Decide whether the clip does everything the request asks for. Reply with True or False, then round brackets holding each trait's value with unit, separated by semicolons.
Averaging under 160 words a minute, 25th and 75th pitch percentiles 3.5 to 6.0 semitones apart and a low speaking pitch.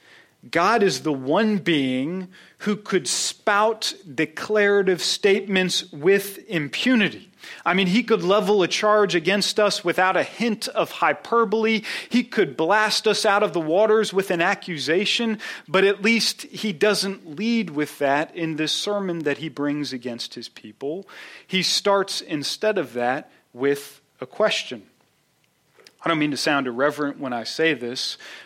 False (150 wpm; 5.4 semitones; 190 Hz)